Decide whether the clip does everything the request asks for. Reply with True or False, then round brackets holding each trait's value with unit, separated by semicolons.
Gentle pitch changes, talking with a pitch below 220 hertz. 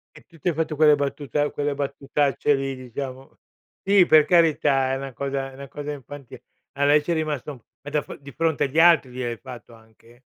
True (2.0 semitones; 140 Hz)